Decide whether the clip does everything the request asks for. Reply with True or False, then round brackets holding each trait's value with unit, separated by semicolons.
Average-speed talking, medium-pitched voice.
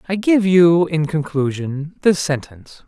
True (145 wpm; 160 Hz)